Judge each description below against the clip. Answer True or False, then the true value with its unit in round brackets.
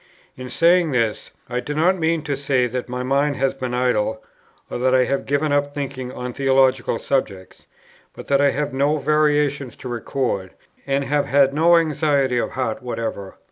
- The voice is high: False (135 Hz)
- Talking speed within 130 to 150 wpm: False (185 wpm)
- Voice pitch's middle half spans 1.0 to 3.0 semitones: True (2.6 semitones)